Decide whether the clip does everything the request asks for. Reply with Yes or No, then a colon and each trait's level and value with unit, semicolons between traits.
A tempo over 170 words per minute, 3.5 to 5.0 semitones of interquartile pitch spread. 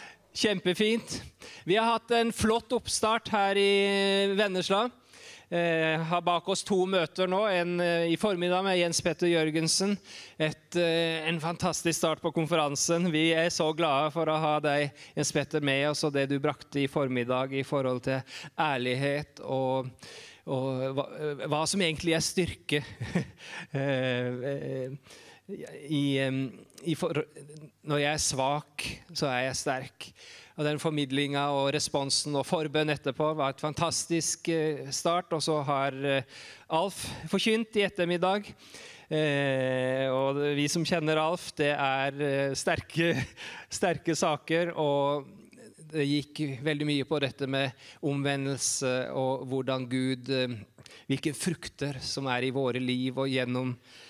No: average, 140 wpm; average, 3.8 semitones